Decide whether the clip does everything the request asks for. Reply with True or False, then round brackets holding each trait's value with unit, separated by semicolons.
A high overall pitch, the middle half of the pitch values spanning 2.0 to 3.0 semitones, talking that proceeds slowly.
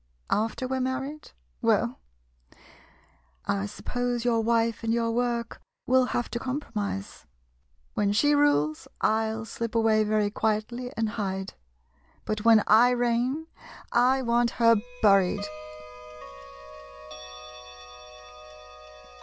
True (230 Hz; 2.5 semitones; 115 wpm)